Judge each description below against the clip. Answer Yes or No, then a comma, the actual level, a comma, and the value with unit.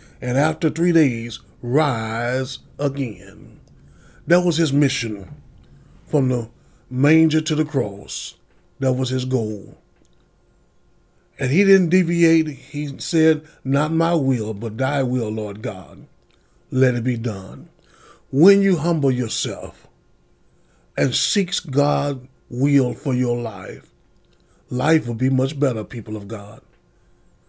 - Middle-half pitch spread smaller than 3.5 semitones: No, average, 4.7 semitones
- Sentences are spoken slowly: Yes, slow, 125 wpm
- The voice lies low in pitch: Yes, low, 130 Hz